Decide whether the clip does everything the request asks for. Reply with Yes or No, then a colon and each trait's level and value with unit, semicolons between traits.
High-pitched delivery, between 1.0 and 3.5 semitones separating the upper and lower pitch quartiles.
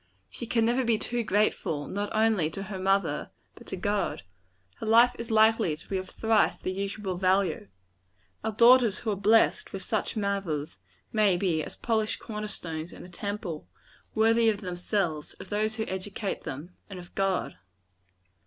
Yes: high, 200 Hz; average, 3.1 semitones